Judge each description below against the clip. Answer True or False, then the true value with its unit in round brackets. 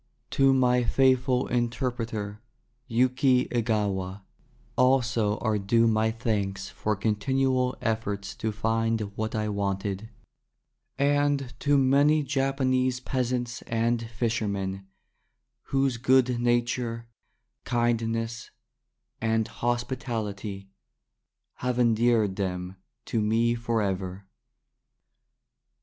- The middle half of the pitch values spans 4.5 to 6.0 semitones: False (3.0 semitones)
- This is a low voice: True (115 Hz)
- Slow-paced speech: True (90 wpm)